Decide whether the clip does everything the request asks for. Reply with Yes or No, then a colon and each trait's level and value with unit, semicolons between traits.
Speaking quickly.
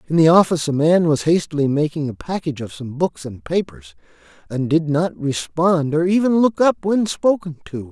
No: average, 195 wpm